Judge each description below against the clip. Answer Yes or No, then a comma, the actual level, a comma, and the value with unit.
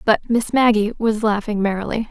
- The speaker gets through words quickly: No, average, 170 wpm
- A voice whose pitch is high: Yes, high, 215 Hz